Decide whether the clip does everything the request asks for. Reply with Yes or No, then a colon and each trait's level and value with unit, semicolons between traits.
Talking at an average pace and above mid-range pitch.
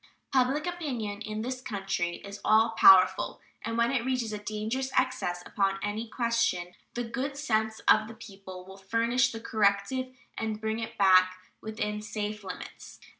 Yes: average, 160 wpm; high, 220 Hz